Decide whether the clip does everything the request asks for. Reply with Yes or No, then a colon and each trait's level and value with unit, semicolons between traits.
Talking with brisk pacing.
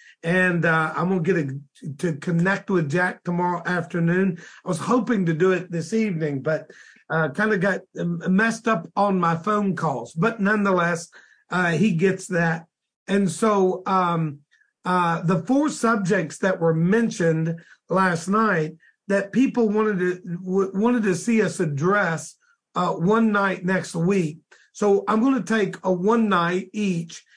No: average, 160 wpm